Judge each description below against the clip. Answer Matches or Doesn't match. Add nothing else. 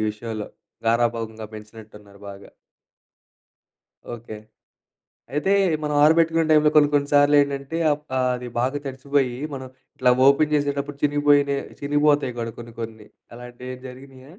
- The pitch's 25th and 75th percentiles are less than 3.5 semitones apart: Doesn't match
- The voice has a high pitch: Doesn't match